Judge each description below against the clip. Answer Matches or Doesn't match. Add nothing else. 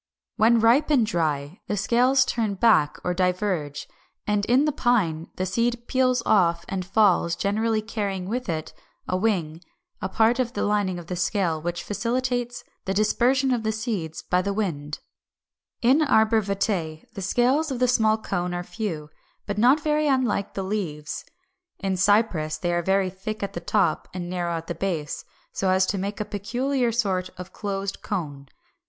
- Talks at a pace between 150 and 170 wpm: Doesn't match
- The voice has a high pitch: Matches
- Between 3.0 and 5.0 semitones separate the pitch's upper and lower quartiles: Matches